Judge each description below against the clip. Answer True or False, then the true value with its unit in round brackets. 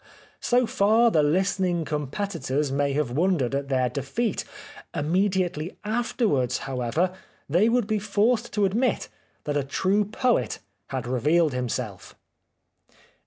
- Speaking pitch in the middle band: True (175 Hz)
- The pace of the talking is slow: True (125 wpm)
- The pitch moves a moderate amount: False (7.0 semitones)